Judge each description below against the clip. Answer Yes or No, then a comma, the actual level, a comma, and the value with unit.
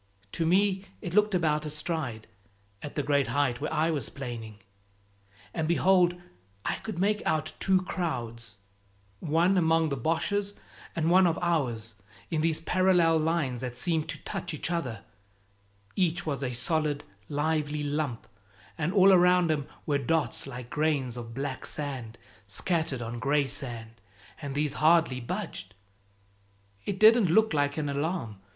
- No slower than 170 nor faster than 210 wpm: No, average, 150 wpm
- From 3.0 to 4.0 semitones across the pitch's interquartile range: No, average, 4.6 semitones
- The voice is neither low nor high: Yes, medium, 155 Hz